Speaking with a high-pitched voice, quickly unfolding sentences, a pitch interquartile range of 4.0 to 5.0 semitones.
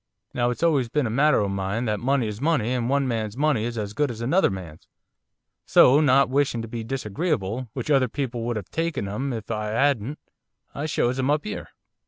No: low, 125 Hz; fast, 215 wpm; average, 4.3 semitones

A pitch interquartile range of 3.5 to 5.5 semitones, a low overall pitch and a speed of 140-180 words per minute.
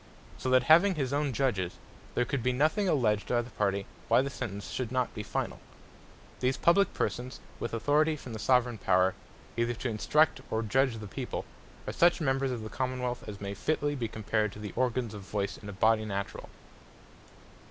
No: average, 4.0 semitones; low, 120 Hz; average, 195 wpm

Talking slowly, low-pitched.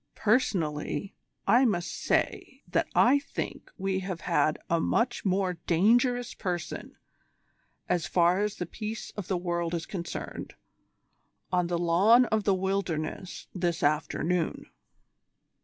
No: slow, 125 wpm; medium, 185 Hz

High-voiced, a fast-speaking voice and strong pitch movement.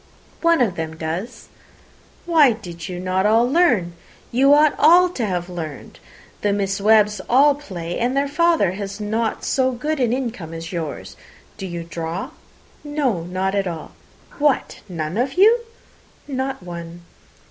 No: high, 210 Hz; average, 155 wpm; wide, 7.7 semitones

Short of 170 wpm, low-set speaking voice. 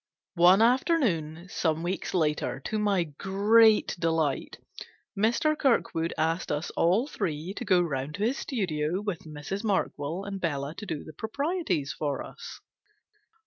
No: average, 145 wpm; medium, 180 Hz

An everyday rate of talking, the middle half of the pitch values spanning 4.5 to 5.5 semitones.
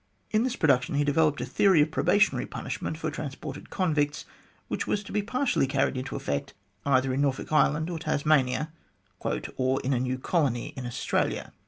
No: average, 180 wpm; average, 3.7 semitones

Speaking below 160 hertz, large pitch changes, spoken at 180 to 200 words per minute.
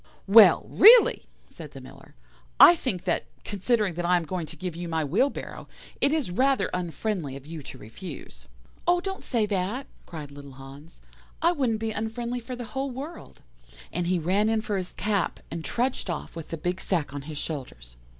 No: medium, 185 Hz; wide, 6.9 semitones; average, 190 wpm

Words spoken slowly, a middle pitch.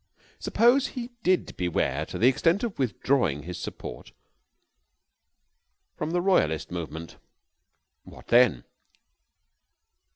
No: slow, 100 wpm; low, 130 Hz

